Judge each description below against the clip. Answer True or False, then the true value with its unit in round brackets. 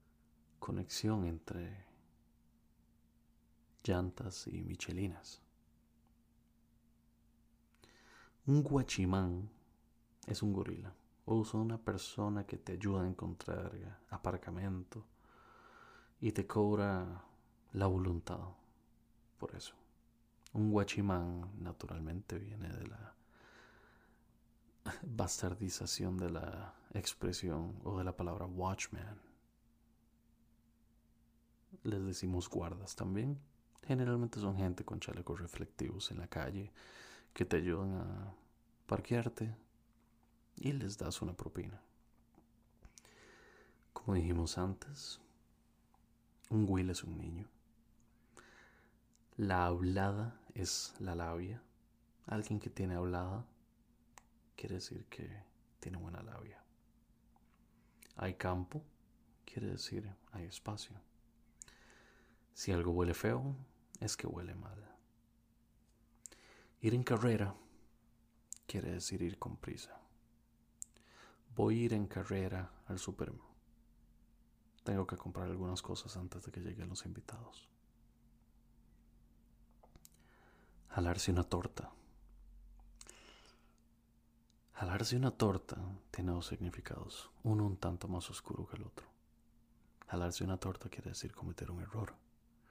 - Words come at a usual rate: False (100 wpm)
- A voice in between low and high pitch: False (105 Hz)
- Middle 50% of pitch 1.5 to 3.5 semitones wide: False (4.1 semitones)